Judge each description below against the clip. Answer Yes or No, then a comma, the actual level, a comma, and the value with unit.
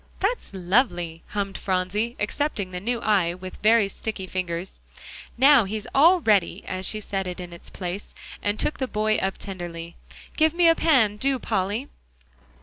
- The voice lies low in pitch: No, high, 205 Hz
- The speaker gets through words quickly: No, average, 165 wpm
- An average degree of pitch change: Yes, average, 4.6 semitones